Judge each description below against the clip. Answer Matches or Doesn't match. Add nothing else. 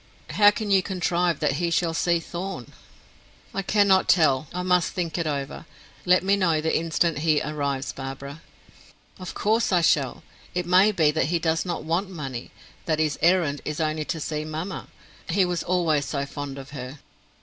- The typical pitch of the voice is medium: Matches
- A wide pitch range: Doesn't match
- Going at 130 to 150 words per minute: Doesn't match